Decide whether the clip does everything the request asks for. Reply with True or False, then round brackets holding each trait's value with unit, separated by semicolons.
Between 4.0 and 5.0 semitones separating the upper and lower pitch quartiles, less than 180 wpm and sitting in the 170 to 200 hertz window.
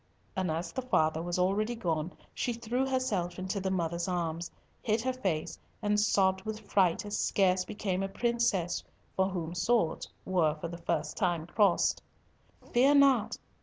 True (4.3 semitones; 165 wpm; 190 Hz)